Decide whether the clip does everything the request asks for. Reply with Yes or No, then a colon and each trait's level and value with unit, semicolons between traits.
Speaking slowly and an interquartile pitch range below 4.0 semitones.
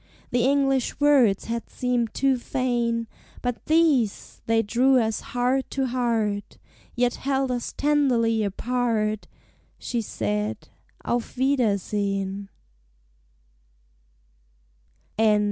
Yes: slow, 95 wpm; average, 3.3 semitones